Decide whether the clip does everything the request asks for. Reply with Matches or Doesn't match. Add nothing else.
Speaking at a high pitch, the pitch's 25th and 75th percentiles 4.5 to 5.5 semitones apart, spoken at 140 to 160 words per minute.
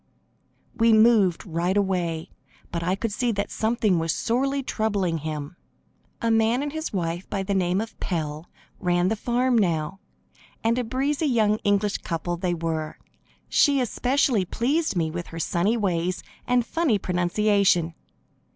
Matches